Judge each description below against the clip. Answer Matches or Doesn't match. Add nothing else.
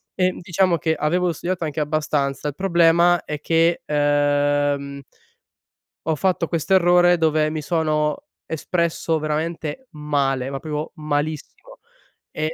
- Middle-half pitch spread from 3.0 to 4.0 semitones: Doesn't match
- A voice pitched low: Doesn't match